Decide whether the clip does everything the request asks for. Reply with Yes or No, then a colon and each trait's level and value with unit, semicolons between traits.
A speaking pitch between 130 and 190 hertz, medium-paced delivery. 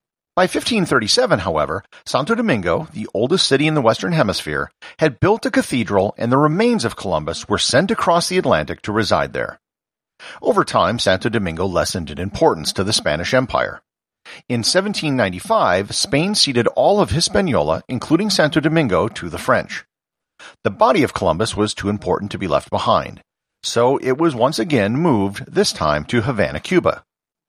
Yes: medium, 140 Hz; average, 165 wpm